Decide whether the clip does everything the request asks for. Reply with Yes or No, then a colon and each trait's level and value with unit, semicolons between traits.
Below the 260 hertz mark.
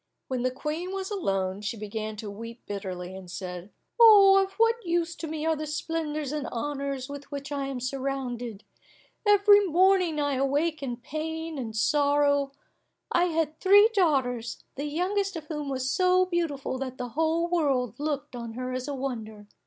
No: very high, 285 Hz